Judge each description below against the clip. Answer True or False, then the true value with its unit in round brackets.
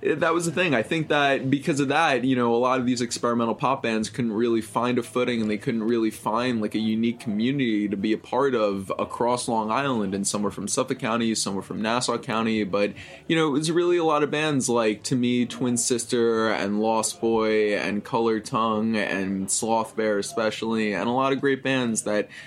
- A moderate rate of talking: False (225 wpm)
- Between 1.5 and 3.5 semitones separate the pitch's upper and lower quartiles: True (3.0 semitones)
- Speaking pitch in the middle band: False (115 Hz)